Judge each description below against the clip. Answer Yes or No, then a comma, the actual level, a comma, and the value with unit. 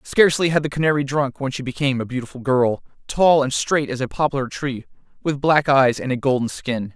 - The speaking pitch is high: No, low, 135 Hz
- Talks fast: Yes, fast, 215 wpm